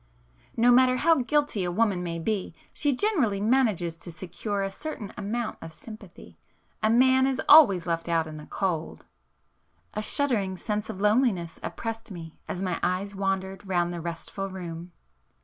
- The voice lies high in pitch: Yes, high, 195 Hz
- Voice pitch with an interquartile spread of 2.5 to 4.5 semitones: No, average, 5.0 semitones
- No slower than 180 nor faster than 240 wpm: No, average, 160 wpm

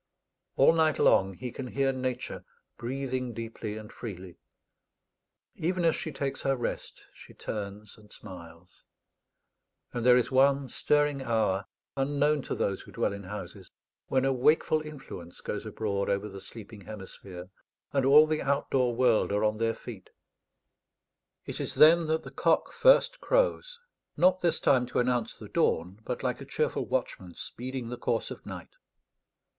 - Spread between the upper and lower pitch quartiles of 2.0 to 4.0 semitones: No, average, 5.1 semitones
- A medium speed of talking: Yes, average, 160 wpm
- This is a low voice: Yes, low, 125 Hz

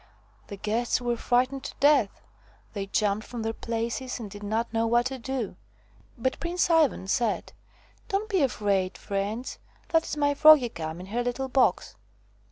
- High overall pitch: Yes, high, 240 Hz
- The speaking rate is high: No, average, 170 wpm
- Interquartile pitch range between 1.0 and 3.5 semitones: No, average, 4.2 semitones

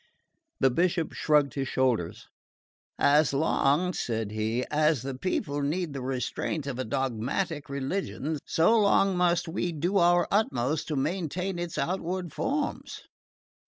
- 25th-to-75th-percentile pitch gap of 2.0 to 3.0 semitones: No, average, 4.8 semitones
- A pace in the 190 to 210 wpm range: No, slow, 135 wpm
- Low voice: No, medium, 150 Hz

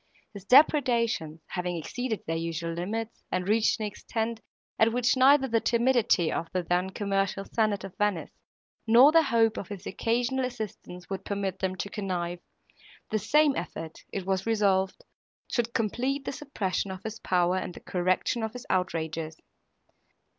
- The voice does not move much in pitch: No, average, 4.3 semitones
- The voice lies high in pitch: Yes, high, 205 Hz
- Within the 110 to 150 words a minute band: No, average, 160 wpm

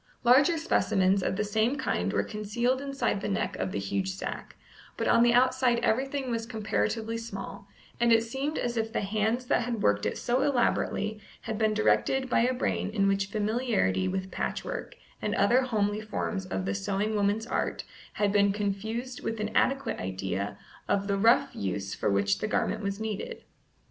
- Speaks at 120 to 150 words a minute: No, average, 185 wpm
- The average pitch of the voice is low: No, high, 215 Hz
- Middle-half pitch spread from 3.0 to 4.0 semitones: Yes, average, 3.4 semitones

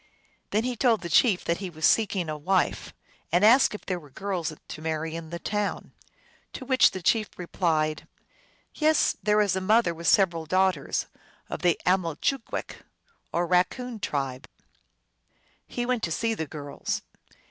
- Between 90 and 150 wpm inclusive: No, average, 165 wpm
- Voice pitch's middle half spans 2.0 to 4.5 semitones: No, average, 4.9 semitones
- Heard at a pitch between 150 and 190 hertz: Yes, medium, 185 Hz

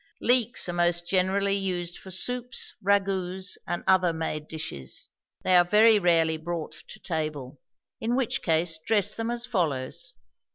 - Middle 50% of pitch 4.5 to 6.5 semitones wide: No, average, 3.9 semitones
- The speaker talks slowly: No, average, 150 wpm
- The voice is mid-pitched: Yes, medium, 180 Hz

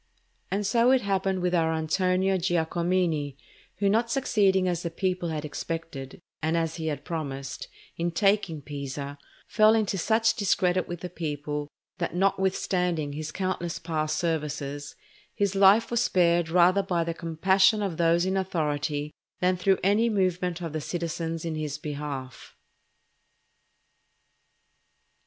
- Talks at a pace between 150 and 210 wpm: No, average, 140 wpm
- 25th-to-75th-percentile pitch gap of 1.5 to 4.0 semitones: Yes, average, 3.5 semitones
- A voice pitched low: No, medium, 175 Hz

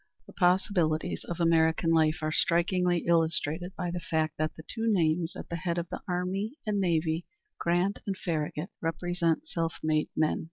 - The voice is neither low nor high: Yes, medium, 170 Hz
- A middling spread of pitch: No, narrow, 2.1 semitones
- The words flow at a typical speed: Yes, average, 170 wpm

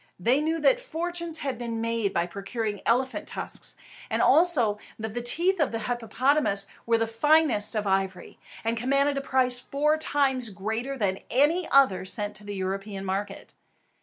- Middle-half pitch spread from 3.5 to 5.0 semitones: No, wide, 5.6 semitones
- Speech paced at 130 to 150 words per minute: No, average, 165 wpm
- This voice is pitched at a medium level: No, high, 235 Hz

